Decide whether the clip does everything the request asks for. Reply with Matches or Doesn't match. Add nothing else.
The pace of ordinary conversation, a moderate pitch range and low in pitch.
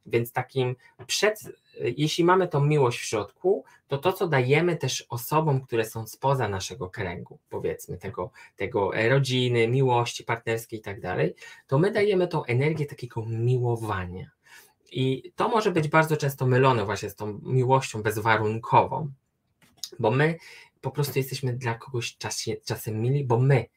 Matches